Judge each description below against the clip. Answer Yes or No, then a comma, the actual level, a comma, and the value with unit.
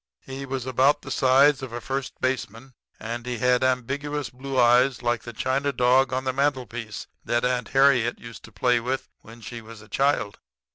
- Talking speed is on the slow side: No, average, 190 wpm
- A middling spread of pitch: No, narrow, 2.1 semitones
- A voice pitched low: Yes, low, 125 Hz